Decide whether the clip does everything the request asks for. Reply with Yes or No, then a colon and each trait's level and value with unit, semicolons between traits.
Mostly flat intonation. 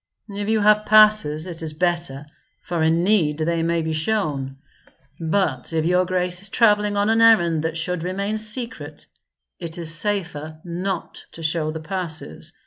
No: average, 4.2 semitones